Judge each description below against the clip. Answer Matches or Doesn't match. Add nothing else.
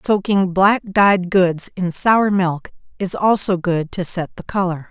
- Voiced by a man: Doesn't match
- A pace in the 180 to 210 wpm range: Doesn't match